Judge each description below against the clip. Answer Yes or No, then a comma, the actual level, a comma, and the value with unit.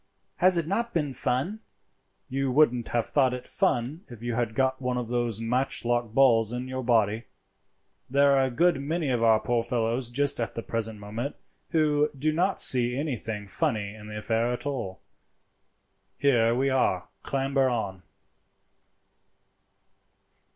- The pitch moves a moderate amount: Yes, average, 3.4 semitones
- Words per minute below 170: Yes, average, 155 wpm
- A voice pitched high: No, low, 125 Hz